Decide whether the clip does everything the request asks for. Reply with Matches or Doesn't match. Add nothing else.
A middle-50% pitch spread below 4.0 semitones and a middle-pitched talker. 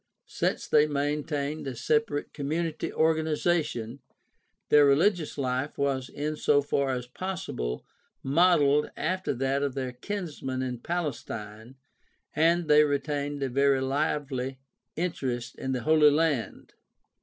Matches